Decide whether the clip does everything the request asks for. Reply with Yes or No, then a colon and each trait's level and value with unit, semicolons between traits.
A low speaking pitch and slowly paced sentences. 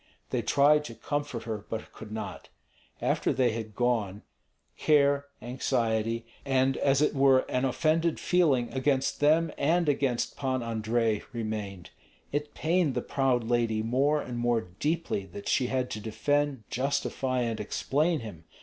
No: low, 130 Hz; average, 150 wpm